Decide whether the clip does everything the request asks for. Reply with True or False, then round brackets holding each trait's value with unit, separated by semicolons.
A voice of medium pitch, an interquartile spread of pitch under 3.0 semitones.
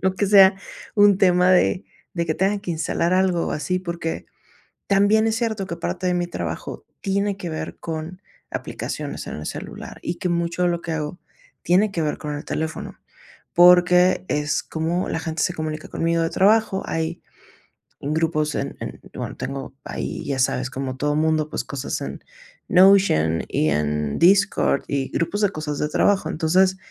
False (170 Hz; 3.7 semitones)